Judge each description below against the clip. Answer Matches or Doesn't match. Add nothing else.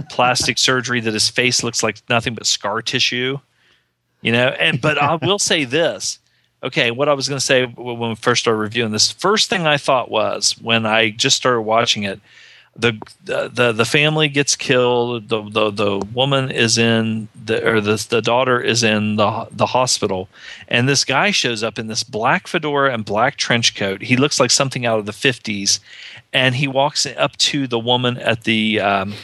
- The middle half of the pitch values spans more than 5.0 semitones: Doesn't match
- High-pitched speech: Doesn't match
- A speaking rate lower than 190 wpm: Doesn't match